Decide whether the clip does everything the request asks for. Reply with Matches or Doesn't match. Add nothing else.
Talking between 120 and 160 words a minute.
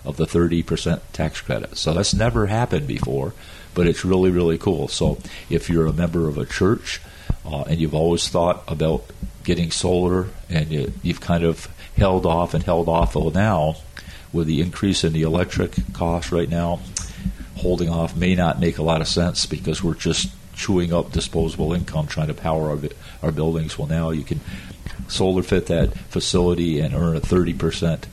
Doesn't match